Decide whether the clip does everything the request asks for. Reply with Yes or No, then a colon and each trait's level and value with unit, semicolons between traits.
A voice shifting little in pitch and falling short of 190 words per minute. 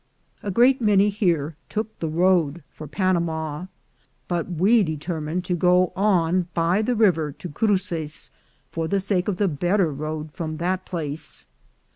No: average, 3.6 semitones; average, 150 wpm